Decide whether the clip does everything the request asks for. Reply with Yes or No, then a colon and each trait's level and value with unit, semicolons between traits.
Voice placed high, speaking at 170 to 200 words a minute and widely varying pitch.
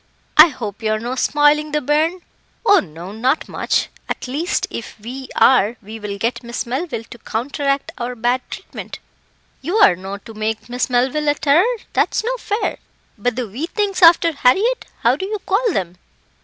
Yes: very high, 260 Hz; average, 175 wpm; wide, 6.5 semitones